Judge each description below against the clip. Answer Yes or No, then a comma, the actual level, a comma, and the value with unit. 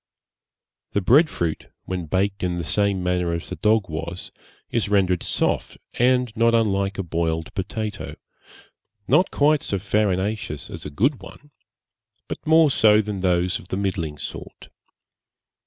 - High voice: No, low, 100 Hz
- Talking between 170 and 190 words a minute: No, average, 150 wpm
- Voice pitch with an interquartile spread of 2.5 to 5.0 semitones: Yes, average, 3.9 semitones